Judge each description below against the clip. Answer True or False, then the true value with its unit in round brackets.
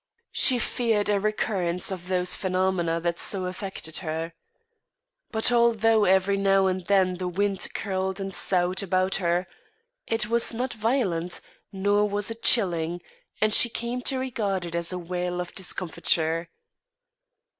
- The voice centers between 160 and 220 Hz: True (190 Hz)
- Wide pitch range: False (3.1 semitones)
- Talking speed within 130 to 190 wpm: True (145 wpm)